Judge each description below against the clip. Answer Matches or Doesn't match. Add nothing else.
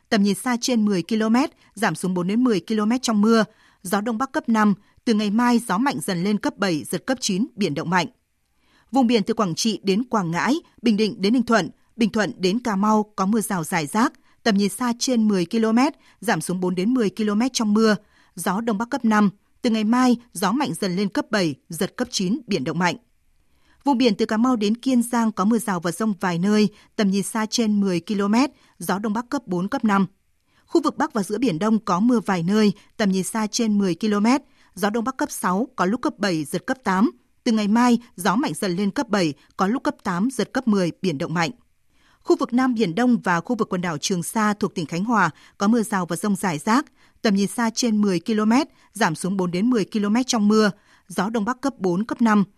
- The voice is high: Matches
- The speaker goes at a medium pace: Matches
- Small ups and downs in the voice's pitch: Doesn't match